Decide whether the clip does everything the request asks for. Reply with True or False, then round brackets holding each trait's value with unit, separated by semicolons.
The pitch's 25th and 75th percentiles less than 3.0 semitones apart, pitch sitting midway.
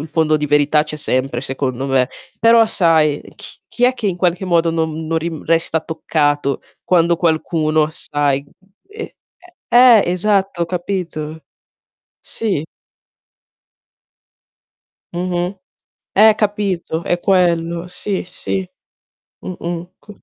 False (3.3 semitones; 170 Hz)